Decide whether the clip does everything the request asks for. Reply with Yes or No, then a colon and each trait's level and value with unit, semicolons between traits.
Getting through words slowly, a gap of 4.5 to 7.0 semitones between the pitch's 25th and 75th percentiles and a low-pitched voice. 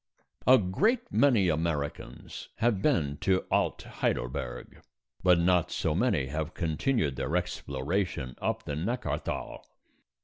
Yes: slow, 115 wpm; wide, 5.6 semitones; very low, 85 Hz